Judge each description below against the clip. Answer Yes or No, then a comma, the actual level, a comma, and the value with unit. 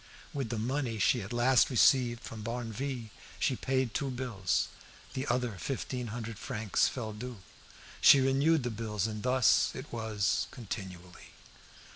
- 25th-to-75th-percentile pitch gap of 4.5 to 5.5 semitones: No, average, 3.1 semitones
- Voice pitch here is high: No, low, 120 Hz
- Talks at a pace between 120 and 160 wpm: Yes, average, 145 wpm